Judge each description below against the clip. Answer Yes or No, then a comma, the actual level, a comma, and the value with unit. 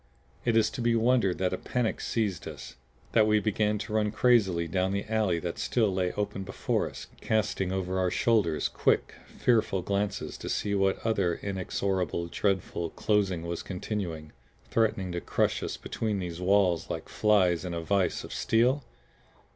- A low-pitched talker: Yes, very low, 95 Hz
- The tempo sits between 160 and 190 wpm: Yes, average, 170 wpm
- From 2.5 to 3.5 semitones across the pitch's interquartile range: Yes, average, 3.2 semitones